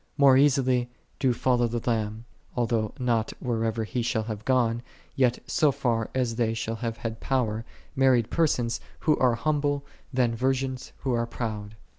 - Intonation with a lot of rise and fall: No, narrow, 2.5 semitones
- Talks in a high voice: No, low, 120 Hz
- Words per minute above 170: No, average, 160 wpm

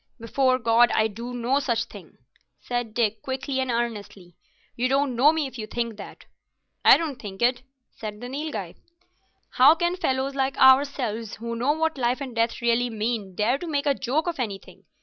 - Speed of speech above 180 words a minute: Yes, average, 190 wpm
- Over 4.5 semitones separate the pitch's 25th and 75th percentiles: No, average, 3.1 semitones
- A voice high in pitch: Yes, high, 245 Hz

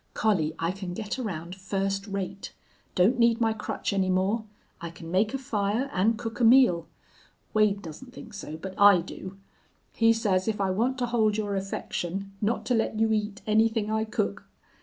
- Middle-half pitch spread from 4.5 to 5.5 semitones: No, average, 3.0 semitones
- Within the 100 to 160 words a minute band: No, average, 185 wpm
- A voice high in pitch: Yes, high, 205 Hz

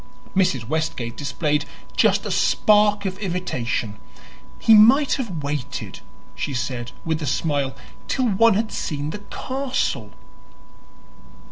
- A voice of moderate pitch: Yes, medium, 160 Hz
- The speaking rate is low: Yes, slow, 120 wpm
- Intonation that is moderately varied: No, wide, 7.1 semitones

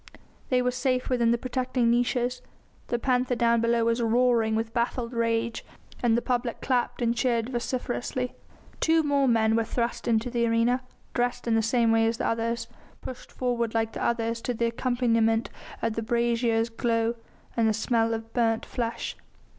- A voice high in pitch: Yes, high, 235 Hz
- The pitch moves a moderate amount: No, narrow, 1.4 semitones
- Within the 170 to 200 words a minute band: Yes, average, 175 wpm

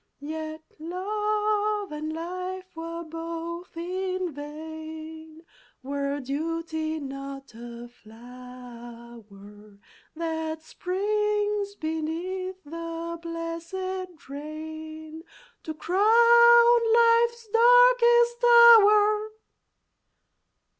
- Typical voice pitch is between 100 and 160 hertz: No, very high, 330 Hz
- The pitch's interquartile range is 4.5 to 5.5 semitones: Yes, average, 5.1 semitones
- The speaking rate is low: Yes, slow, 70 wpm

